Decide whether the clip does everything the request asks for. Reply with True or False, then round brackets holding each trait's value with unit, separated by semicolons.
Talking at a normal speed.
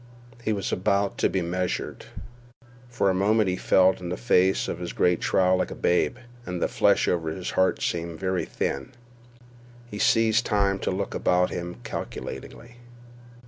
True (170 wpm)